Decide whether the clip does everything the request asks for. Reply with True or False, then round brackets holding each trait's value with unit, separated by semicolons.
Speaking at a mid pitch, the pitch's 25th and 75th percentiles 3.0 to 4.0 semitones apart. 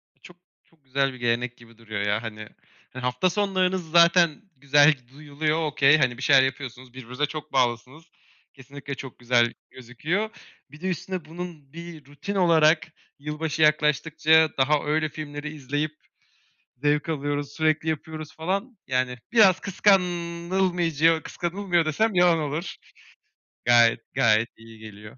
False (150 Hz; 4.6 semitones)